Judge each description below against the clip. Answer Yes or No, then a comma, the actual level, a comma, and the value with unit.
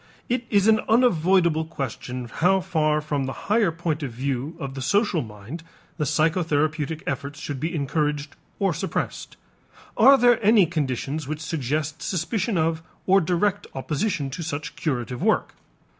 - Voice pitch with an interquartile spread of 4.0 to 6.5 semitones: Yes, average, 4.4 semitones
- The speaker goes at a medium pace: Yes, average, 150 wpm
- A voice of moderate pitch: Yes, medium, 155 Hz